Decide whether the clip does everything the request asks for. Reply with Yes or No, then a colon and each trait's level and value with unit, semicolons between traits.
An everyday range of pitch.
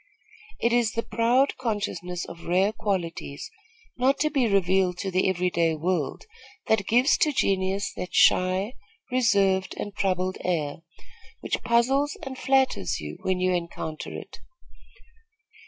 Yes: average, 4.7 semitones